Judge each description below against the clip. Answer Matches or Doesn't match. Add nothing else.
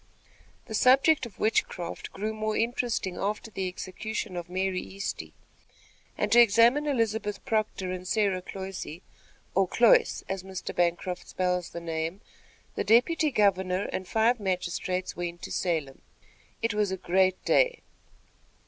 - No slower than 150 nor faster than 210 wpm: Doesn't match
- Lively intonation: Doesn't match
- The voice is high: Matches